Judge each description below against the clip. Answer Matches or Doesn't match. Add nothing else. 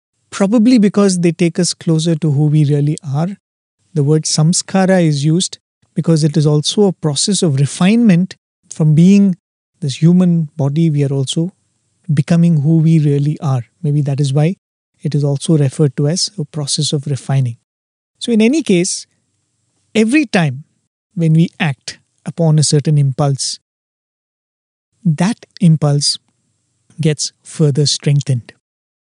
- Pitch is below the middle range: Doesn't match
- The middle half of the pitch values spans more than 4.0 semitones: Doesn't match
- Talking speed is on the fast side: Doesn't match